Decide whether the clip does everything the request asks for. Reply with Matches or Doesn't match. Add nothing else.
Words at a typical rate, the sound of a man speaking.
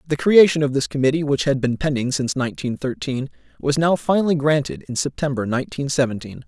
Matches